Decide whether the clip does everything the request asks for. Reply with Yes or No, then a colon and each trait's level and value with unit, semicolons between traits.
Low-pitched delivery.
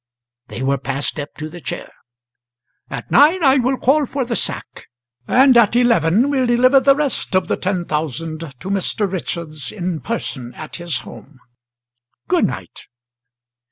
No: medium, 185 Hz